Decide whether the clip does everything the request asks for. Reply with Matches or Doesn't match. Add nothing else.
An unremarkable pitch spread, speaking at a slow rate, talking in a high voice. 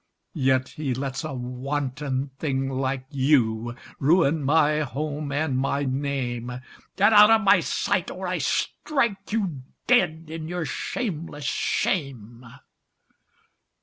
Doesn't match